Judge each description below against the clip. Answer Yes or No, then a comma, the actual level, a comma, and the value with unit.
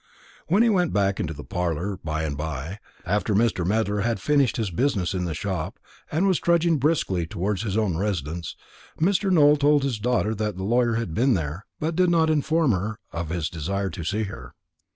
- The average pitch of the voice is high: No, low, 105 Hz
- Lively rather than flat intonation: Yes, wide, 8.4 semitones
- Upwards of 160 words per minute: Yes, average, 200 wpm